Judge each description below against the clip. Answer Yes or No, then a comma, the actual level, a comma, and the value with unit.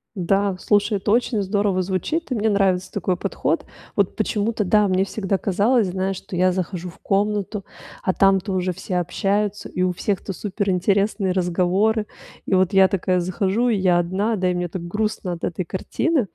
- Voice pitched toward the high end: Yes, high, 195 Hz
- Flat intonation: Yes, narrow, 2.2 semitones